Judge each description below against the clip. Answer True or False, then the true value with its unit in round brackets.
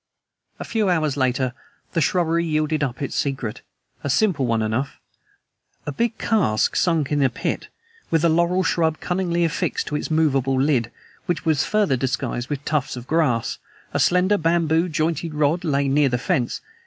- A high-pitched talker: False (150 Hz)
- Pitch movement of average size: True (4.0 semitones)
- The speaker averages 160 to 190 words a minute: True (170 wpm)